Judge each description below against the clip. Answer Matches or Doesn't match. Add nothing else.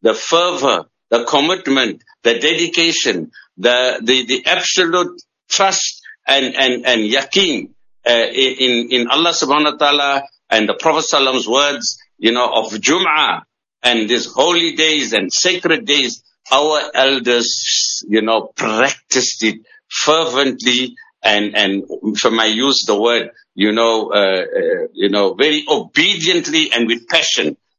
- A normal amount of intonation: Doesn't match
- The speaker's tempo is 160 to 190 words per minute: Doesn't match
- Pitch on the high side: Doesn't match